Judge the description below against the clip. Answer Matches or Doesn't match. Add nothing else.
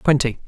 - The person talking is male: Matches